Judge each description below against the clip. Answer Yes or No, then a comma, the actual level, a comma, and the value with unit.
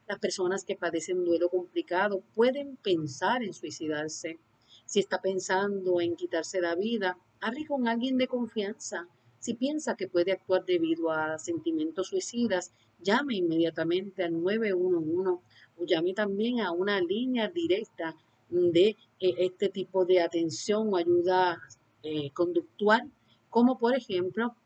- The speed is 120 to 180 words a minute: Yes, average, 135 wpm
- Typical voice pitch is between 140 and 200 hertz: Yes, medium, 185 Hz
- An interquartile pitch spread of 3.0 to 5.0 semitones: Yes, average, 4.0 semitones